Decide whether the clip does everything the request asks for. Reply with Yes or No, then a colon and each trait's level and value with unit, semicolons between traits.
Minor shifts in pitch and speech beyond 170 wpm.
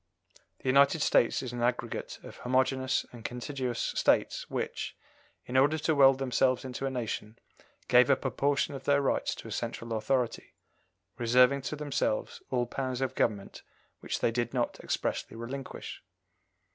No: narrow, 2.1 semitones; average, 160 wpm